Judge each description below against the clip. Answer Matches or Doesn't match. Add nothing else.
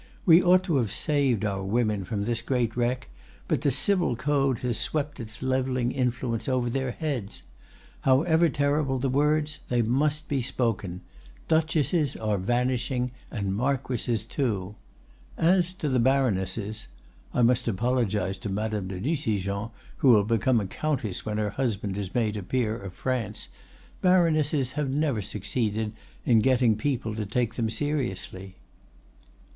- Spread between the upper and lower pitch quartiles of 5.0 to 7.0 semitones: Doesn't match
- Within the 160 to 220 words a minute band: Doesn't match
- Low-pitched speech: Matches